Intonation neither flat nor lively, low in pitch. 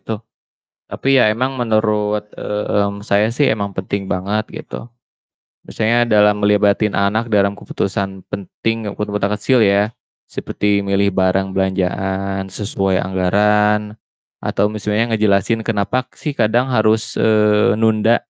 No: narrow, 1.7 semitones; low, 105 Hz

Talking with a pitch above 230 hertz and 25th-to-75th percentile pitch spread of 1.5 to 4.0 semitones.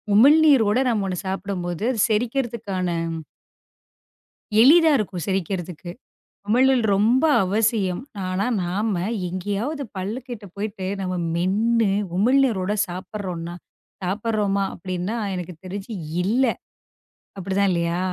No: high, 200 Hz; average, 3.7 semitones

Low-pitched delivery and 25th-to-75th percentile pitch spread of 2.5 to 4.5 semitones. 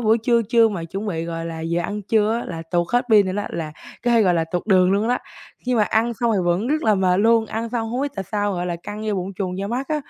No: high, 205 Hz; average, 4.2 semitones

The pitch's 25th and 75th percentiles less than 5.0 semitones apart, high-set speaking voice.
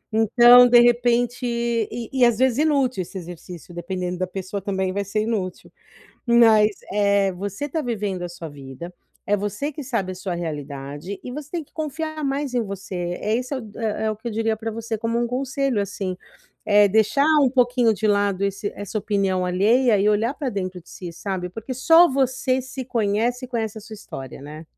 Yes: average, 4.5 semitones; high, 220 Hz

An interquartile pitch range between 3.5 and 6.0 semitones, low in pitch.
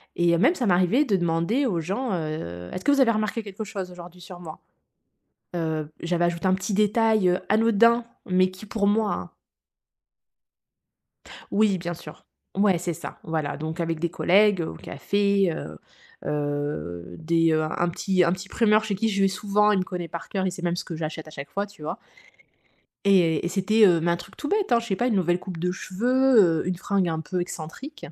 No: average, 3.9 semitones; medium, 185 Hz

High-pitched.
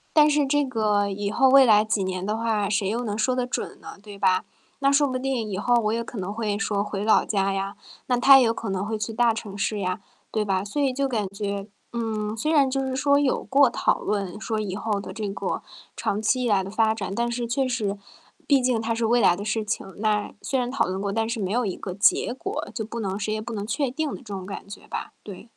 Yes: high, 220 Hz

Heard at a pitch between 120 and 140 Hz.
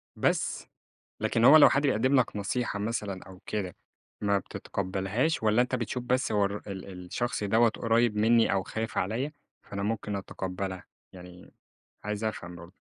No: low, 105 Hz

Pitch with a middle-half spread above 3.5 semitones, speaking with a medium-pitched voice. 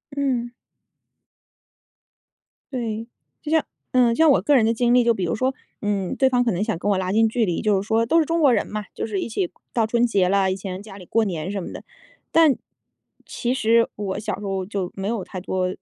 No: average, 3.9 semitones; high, 220 Hz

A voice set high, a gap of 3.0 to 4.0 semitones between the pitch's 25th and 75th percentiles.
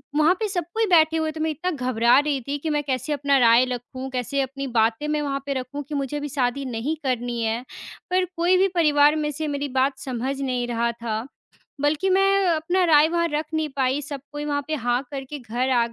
Yes: very high, 280 Hz; average, 3.5 semitones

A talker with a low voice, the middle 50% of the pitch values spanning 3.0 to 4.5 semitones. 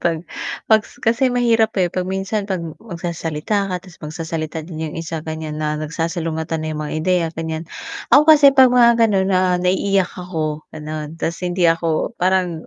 No: medium, 175 Hz; average, 3.7 semitones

